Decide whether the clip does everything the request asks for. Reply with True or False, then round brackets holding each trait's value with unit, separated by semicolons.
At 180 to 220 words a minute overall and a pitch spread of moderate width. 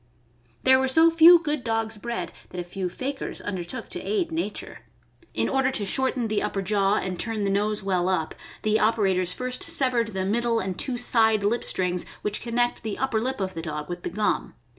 True (205 wpm; 4.9 semitones)